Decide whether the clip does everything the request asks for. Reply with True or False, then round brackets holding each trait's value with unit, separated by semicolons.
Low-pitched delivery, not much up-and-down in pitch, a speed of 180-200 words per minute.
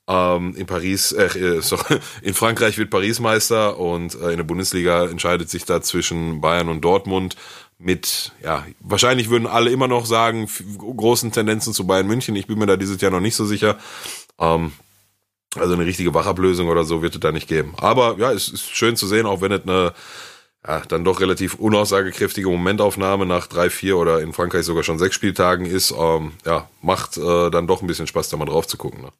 False (95 Hz; 3.5 semitones; 185 wpm)